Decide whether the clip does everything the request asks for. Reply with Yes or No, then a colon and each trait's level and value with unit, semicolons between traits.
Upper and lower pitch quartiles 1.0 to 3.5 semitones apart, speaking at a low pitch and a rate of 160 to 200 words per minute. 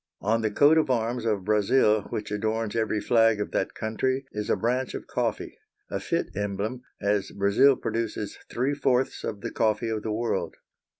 Yes: average, 2.9 semitones; low, 110 Hz; average, 180 wpm